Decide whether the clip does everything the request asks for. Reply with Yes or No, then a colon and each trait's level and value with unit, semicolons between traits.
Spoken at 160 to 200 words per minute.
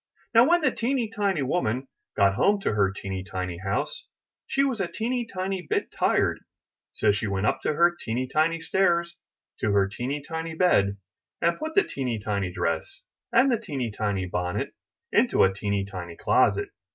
Yes: average, 175 wpm